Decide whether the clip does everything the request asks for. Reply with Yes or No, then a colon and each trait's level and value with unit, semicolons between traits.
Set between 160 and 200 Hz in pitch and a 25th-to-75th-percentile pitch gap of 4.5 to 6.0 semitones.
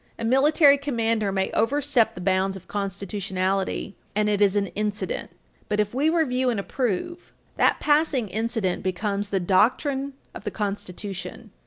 No: high, 210 Hz; average, 4.9 semitones